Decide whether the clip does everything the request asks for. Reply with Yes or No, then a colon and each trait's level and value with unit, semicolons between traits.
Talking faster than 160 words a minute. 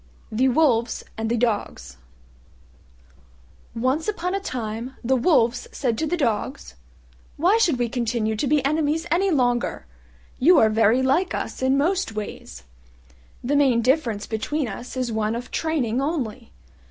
No: average, 150 wpm